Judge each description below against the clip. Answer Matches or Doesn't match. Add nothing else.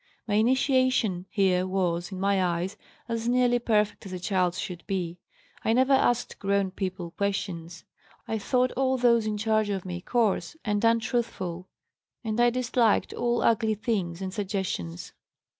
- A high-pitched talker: Matches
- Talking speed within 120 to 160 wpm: Matches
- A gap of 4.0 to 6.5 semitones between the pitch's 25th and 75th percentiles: Matches